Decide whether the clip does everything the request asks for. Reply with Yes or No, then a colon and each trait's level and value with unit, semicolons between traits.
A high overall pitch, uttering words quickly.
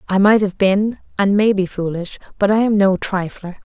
Yes: high, 200 Hz; fast, 210 wpm